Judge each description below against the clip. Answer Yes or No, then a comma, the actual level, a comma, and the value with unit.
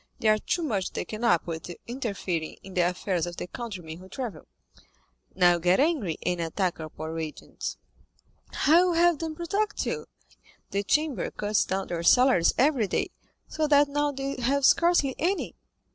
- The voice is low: No, high, 220 Hz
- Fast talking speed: No, average, 175 wpm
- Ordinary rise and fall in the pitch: No, wide, 8.7 semitones